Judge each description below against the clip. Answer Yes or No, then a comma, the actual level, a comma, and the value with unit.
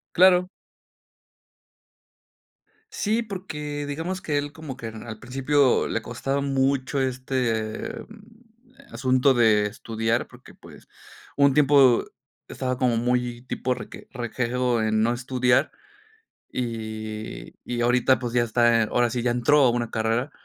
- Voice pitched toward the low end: Yes, low, 125 Hz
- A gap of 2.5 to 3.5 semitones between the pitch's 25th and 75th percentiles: Yes, average, 2.9 semitones